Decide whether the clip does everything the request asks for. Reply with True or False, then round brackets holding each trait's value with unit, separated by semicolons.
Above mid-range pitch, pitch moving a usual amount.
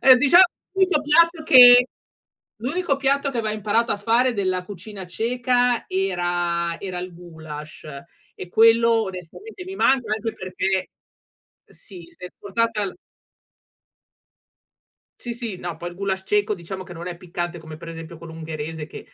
False (200 Hz; 5.8 semitones)